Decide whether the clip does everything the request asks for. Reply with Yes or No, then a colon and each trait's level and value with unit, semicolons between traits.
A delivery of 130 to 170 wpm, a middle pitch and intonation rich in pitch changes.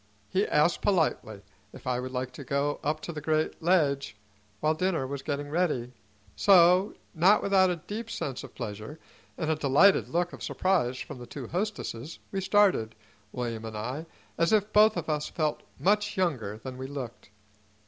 No: average, 180 wpm; medium, 155 Hz; wide, 6.0 semitones